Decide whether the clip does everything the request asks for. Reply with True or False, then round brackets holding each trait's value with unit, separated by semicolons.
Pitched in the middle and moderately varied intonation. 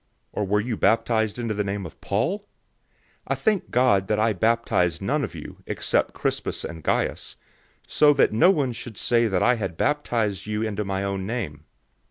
False (110 Hz; 3.6 semitones)